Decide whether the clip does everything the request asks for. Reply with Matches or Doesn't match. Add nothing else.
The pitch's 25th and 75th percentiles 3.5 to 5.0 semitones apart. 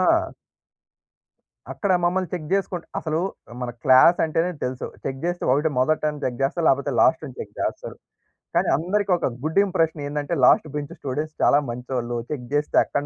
Matches